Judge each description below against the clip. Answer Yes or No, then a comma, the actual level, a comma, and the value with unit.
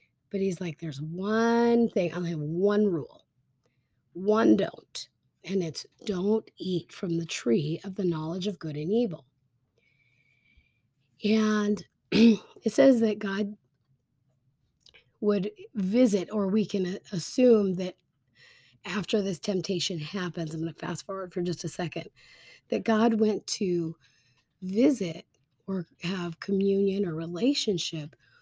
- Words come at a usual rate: No, slow, 130 wpm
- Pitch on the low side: No, medium, 180 Hz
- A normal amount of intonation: Yes, average, 5.0 semitones